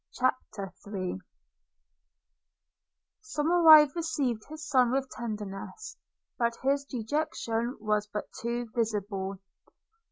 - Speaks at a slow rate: Yes, slow, 90 wpm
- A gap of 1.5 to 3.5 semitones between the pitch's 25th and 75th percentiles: No, average, 5.2 semitones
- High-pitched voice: Yes, high, 235 Hz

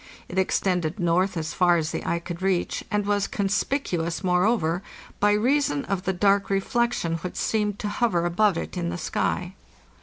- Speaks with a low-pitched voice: No, medium, 185 Hz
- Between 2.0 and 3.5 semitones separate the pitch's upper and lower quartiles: Yes, average, 3.1 semitones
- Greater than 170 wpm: Yes, average, 180 wpm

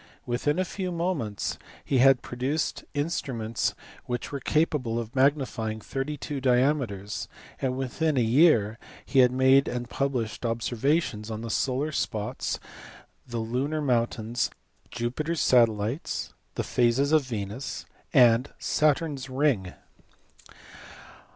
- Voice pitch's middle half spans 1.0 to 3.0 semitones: No, average, 3.8 semitones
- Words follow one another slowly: Yes, slow, 125 wpm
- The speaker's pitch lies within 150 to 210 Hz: No, low, 130 Hz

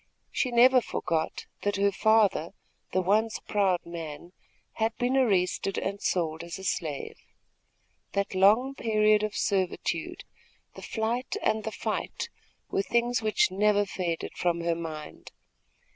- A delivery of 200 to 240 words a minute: No, slow, 135 wpm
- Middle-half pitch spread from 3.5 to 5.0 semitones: Yes, average, 4.0 semitones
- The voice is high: Yes, high, 200 Hz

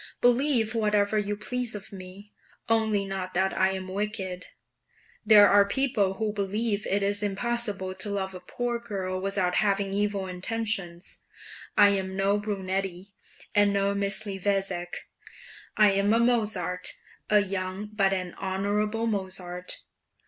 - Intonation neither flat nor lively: No, narrow, 1.9 semitones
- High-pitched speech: Yes, high, 200 Hz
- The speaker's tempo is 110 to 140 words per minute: Yes, slow, 135 wpm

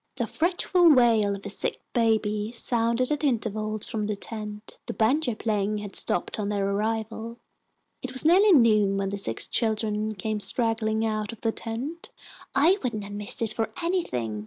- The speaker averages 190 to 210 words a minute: No, average, 175 wpm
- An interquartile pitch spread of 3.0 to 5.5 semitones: No, narrow, 2.4 semitones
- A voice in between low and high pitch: No, high, 220 Hz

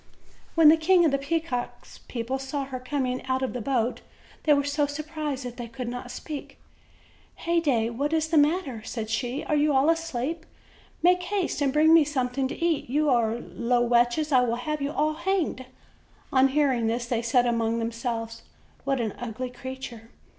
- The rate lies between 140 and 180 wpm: No, average, 190 wpm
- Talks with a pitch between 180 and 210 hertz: No, very high, 265 Hz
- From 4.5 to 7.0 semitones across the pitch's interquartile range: No, average, 4.0 semitones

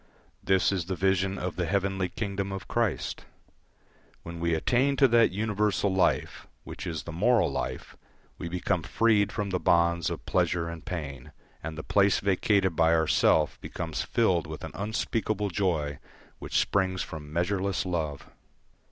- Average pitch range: Yes, average, 3.3 semitones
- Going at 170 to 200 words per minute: No, average, 160 wpm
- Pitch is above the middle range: No, very low, 95 Hz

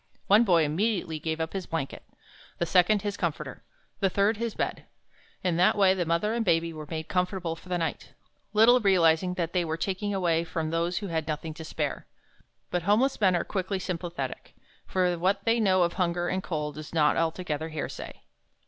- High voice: No, medium, 175 Hz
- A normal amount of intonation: Yes, average, 3.1 semitones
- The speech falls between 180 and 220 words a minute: Yes, average, 195 wpm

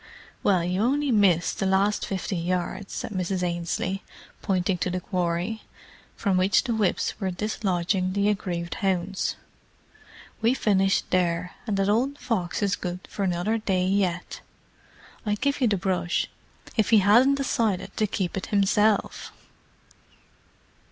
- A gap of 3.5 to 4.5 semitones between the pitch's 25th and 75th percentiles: No, average, 2.7 semitones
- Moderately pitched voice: No, high, 195 Hz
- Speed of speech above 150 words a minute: No, average, 145 wpm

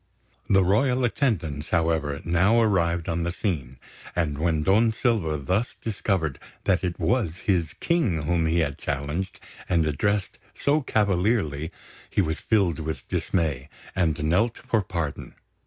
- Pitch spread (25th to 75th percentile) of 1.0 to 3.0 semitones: No, average, 4.7 semitones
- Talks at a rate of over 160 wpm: No, average, 140 wpm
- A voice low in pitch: Yes, very low, 85 Hz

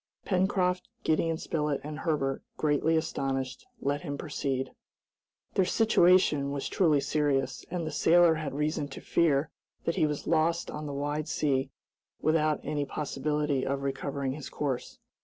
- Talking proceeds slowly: No, average, 145 wpm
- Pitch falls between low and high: Yes, medium, 150 Hz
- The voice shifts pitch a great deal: No, narrow, 2.6 semitones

